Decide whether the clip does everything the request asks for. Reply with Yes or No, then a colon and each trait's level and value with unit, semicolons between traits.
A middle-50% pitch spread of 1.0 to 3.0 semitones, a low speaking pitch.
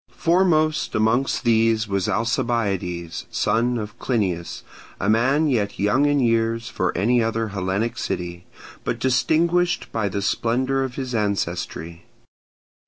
No: average, 4.5 semitones; low, 115 Hz